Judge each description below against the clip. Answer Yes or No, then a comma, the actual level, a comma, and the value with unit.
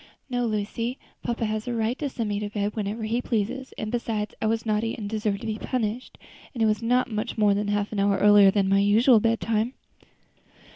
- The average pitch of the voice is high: Yes, high, 215 Hz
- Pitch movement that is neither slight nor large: No, narrow, 2.0 semitones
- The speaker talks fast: Yes, fast, 220 wpm